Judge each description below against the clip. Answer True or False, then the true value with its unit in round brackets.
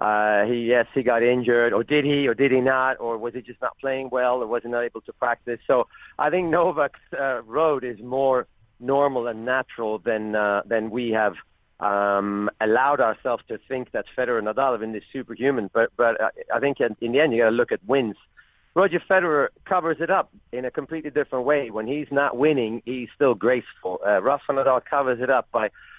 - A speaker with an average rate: False (215 wpm)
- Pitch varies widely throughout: False (3.3 semitones)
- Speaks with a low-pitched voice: True (125 Hz)